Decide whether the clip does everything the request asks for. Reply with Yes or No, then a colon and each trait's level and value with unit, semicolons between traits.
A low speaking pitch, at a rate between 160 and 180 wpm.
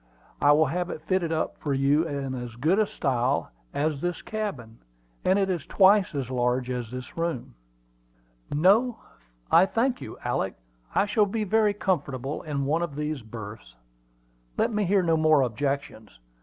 No: medium, 150 Hz; average, 165 wpm